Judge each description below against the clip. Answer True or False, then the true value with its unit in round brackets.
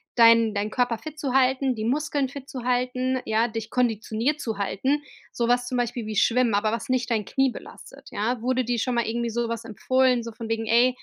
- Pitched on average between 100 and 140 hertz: False (240 Hz)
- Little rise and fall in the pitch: True (2.2 semitones)